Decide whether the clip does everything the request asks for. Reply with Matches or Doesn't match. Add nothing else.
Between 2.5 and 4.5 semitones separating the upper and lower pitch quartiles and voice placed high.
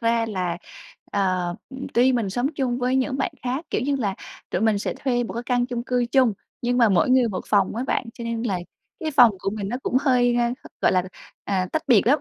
Matches